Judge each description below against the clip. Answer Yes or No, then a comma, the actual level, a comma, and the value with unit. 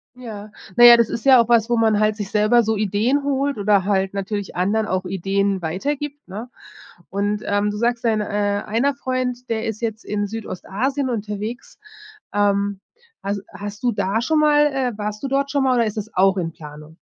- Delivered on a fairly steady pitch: No, average, 3.1 semitones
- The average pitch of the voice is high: Yes, high, 215 Hz